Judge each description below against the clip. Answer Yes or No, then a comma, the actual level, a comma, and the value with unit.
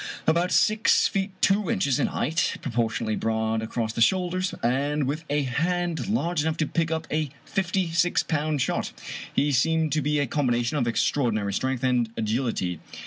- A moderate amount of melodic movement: No, wide, 5.8 semitones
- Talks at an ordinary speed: Yes, average, 175 wpm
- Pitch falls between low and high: Yes, medium, 145 Hz